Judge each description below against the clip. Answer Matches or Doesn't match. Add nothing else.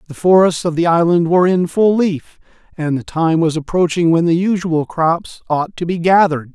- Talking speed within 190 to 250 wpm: Matches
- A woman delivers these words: Doesn't match